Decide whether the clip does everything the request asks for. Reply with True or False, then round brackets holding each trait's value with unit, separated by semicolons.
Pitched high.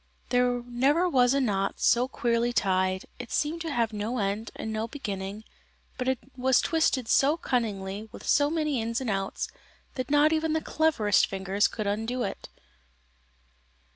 True (240 Hz)